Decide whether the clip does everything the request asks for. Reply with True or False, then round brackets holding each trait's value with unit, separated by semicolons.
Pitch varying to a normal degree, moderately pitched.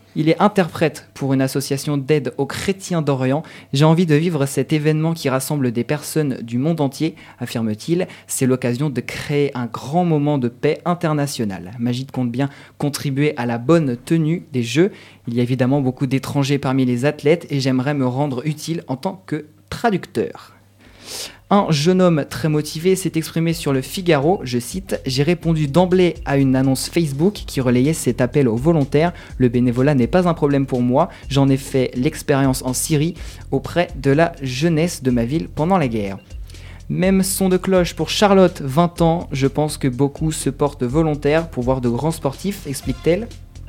True (3.9 semitones; 145 Hz)